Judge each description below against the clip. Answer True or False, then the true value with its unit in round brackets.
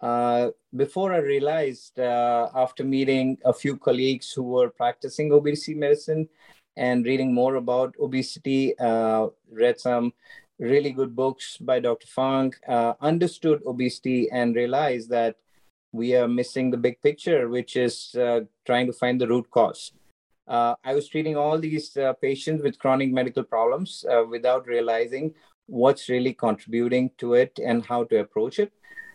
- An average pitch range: True (3.2 semitones)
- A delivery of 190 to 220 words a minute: False (155 wpm)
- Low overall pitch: True (130 Hz)